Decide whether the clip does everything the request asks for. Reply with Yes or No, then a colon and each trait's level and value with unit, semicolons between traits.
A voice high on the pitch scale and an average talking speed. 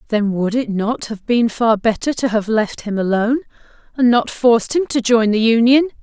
No: high, 230 Hz; fast, 210 wpm